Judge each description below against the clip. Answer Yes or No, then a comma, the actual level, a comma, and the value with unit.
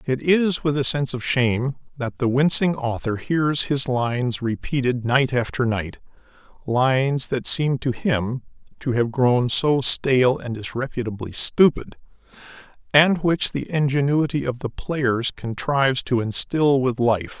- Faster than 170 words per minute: No, average, 145 wpm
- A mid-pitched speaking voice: No, low, 130 Hz